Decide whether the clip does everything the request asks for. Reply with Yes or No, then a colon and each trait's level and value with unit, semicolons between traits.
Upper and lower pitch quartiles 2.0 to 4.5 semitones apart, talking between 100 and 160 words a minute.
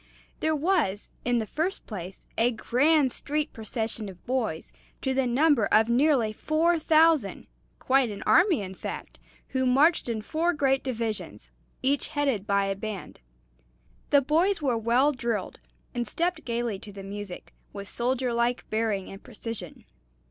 No: wide, 5.6 semitones; average, 155 wpm